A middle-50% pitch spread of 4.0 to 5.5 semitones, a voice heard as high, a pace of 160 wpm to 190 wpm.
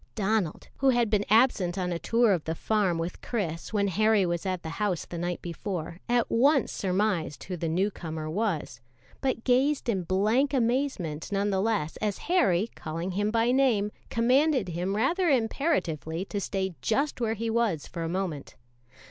Yes: average, 5.1 semitones; high, 200 Hz; average, 180 wpm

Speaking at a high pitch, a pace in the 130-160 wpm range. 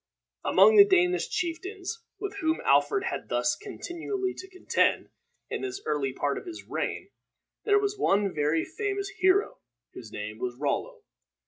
Yes: very high, 370 Hz; average, 150 wpm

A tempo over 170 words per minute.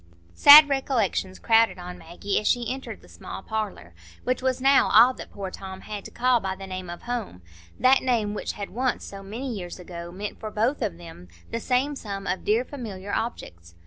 Yes: average, 200 wpm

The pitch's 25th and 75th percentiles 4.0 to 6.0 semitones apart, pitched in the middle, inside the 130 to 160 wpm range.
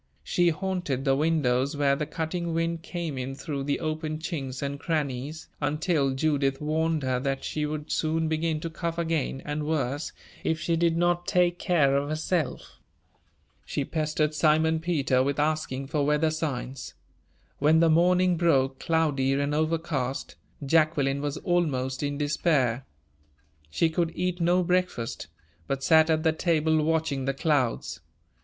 No: average, 3.0 semitones; medium, 155 Hz; average, 150 wpm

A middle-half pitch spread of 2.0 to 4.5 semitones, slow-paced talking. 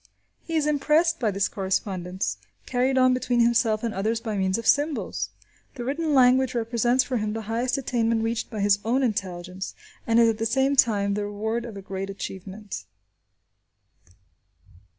No: average, 4.0 semitones; average, 170 wpm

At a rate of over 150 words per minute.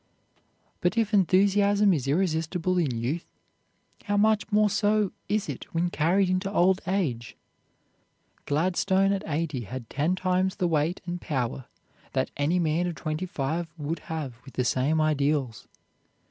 No: average, 145 wpm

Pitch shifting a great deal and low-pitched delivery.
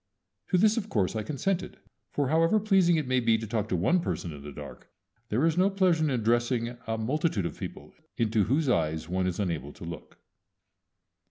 Yes: wide, 9.0 semitones; low, 120 Hz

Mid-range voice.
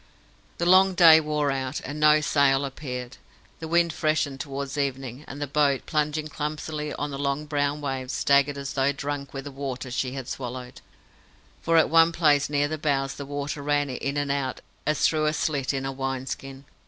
Yes: medium, 145 Hz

